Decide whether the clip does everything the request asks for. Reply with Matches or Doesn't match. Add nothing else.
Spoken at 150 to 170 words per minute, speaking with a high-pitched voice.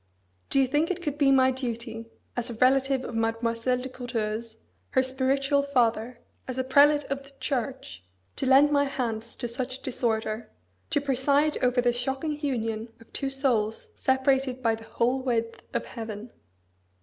Matches